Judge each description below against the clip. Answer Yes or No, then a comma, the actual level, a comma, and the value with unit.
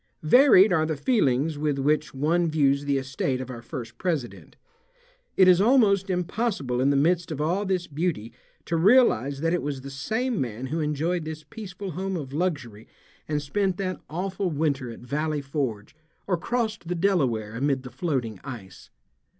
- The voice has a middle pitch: Yes, medium, 155 Hz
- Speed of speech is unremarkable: Yes, average, 175 wpm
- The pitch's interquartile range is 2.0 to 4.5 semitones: No, average, 5.3 semitones